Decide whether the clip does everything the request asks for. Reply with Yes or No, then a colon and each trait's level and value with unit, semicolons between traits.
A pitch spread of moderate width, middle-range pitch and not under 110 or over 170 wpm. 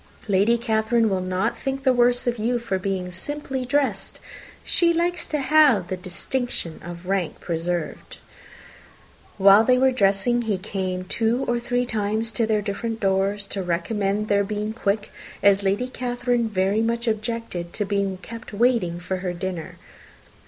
No: average, 4.1 semitones; high, 215 Hz; average, 160 wpm